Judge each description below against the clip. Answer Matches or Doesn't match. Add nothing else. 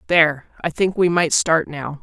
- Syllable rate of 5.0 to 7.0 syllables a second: Doesn't match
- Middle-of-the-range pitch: Matches